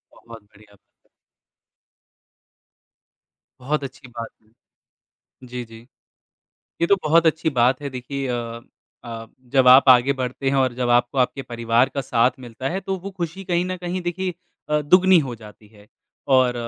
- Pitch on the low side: Yes, low, 130 Hz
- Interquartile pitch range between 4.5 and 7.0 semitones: Yes, average, 5.0 semitones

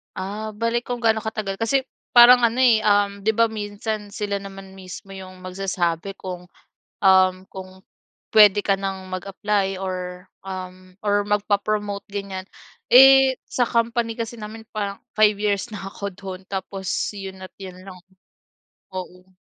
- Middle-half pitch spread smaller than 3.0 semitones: Yes, narrow, 2.4 semitones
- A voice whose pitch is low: No, high, 200 Hz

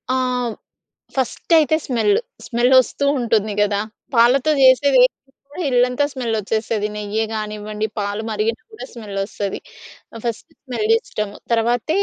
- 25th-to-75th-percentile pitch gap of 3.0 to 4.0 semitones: Yes, average, 3.4 semitones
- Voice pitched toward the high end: Yes, high, 235 Hz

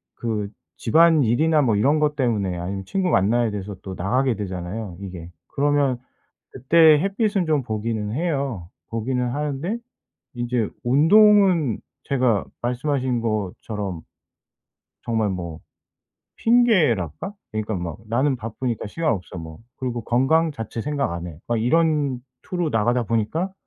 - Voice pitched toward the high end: No, low, 120 Hz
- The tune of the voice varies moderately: No, wide, 6.2 semitones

